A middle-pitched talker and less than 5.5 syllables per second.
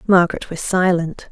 Yes: medium, 180 Hz; 5.1 syllables/s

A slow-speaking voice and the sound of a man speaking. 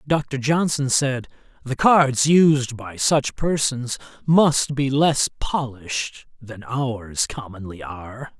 Yes: slow, 120 wpm; male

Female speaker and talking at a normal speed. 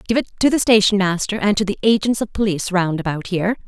No: female; fast, 245 wpm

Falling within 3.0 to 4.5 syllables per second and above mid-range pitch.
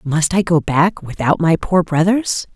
No: 4.2 syllables/s; medium, 170 Hz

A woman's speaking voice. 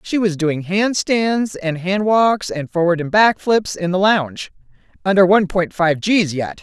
Yes: female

